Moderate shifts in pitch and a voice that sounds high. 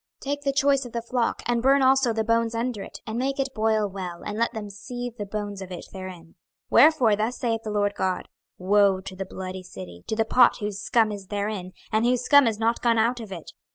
Yes: average, 3.5 semitones; high, 220 Hz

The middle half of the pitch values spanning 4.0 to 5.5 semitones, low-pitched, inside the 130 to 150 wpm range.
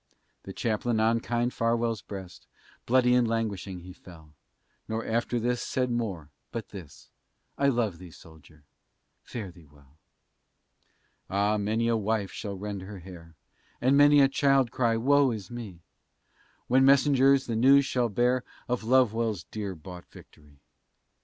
Yes: average, 4.5 semitones; low, 115 Hz; average, 145 wpm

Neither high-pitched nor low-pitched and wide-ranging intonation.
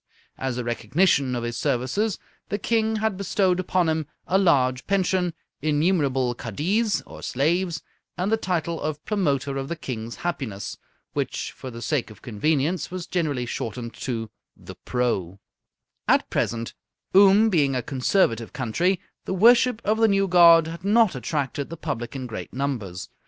Yes: medium, 155 Hz; wide, 6.9 semitones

